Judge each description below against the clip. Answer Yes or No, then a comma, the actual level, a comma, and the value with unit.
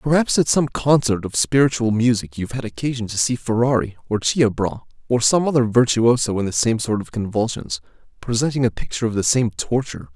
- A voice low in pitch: Yes, low, 115 Hz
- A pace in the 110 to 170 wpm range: No, average, 190 wpm